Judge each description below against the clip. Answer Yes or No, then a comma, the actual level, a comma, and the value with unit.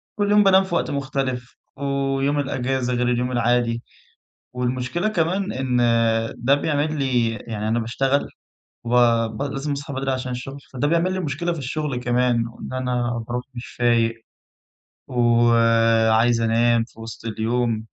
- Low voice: Yes, low, 125 Hz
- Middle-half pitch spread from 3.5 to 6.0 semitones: No, average, 3.1 semitones